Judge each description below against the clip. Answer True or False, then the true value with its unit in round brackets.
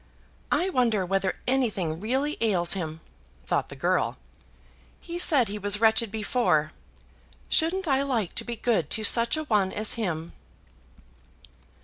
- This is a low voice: False (220 Hz)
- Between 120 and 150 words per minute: True (140 wpm)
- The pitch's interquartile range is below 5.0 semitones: False (5.3 semitones)